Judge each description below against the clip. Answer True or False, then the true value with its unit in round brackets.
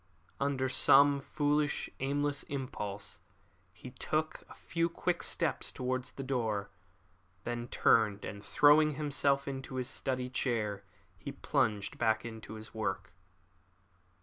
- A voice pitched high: False (130 Hz)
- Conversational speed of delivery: False (125 wpm)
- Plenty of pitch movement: False (4.2 semitones)